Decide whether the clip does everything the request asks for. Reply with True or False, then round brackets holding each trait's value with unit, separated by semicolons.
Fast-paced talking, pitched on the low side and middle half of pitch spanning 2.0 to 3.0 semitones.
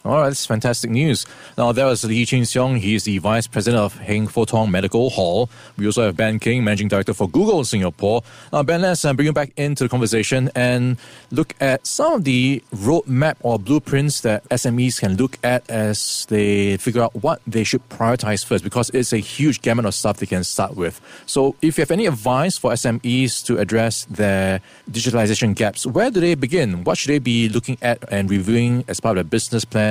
False (215 wpm; 120 Hz; 3.4 semitones)